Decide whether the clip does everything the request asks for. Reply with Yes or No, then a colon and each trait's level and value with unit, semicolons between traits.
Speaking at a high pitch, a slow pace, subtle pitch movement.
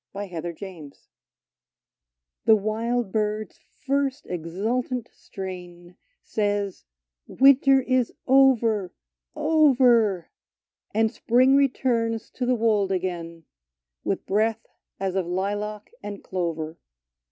No: high, 210 Hz; slow, 105 wpm; average, 5.1 semitones